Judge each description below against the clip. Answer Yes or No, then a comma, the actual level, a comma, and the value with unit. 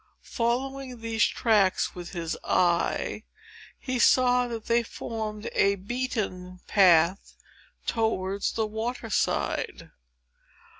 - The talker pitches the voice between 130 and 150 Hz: No, high, 220 Hz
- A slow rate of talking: Yes, slow, 100 wpm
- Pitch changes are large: No, average, 4.1 semitones